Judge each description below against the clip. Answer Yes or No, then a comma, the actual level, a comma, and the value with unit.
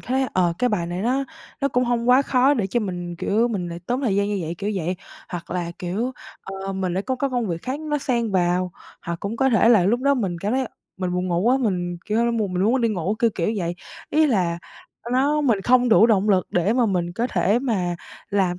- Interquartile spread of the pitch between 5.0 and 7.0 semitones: Yes, wide, 5.5 semitones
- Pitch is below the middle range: No, high, 210 Hz